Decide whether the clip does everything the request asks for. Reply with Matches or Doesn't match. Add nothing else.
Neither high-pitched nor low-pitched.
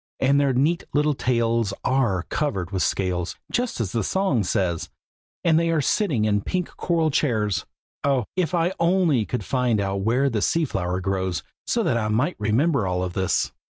Doesn't match